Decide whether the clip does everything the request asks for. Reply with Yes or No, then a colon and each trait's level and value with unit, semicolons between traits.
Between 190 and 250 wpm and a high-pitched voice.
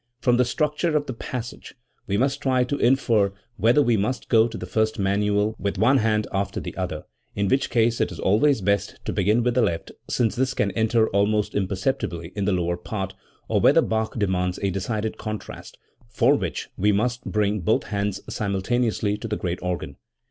No: average, 195 wpm; low, 110 Hz